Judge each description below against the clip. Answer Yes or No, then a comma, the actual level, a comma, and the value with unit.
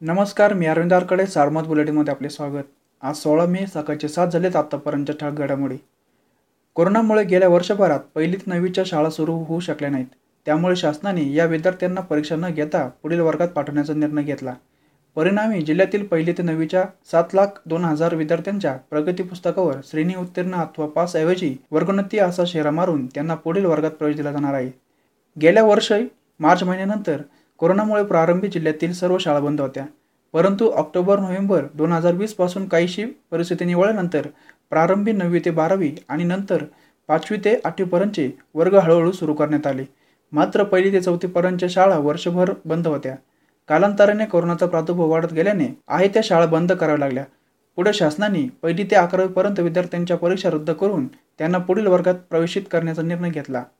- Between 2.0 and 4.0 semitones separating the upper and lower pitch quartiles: Yes, average, 3.4 semitones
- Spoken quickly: Yes, fast, 150 wpm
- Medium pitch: Yes, medium, 170 Hz